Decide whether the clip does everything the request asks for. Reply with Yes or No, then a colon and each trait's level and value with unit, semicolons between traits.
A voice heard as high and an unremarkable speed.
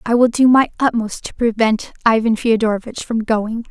Yes: high, 230 Hz; average, 180 wpm